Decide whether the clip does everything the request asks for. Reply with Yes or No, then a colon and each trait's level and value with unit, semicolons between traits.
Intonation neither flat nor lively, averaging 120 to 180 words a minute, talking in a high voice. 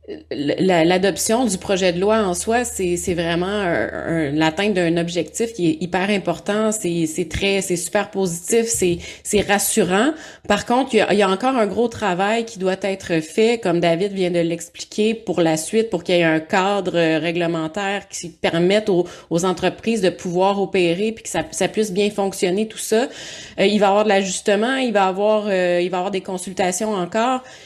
No: average, 3.2 semitones; average, 200 wpm; high, 195 Hz